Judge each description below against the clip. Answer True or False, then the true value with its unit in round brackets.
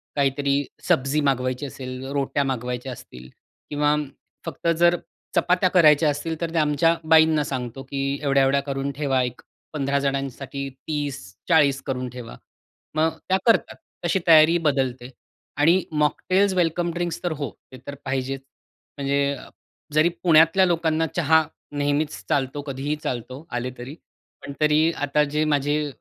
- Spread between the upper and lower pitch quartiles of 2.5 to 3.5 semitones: True (2.8 semitones)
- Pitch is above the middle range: False (145 Hz)